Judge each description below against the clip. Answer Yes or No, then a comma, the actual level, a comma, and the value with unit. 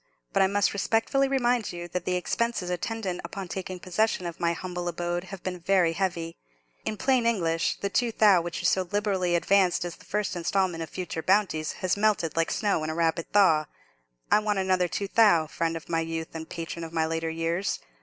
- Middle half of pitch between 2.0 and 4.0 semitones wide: Yes, average, 3.4 semitones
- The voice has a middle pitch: Yes, medium, 180 Hz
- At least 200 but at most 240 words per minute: Yes, fast, 205 wpm